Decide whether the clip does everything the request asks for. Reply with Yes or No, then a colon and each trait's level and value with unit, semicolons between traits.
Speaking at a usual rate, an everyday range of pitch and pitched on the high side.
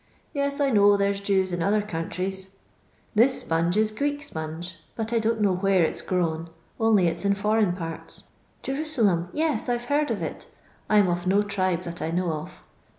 No: fast, 210 wpm; average, 4.1 semitones; high, 200 Hz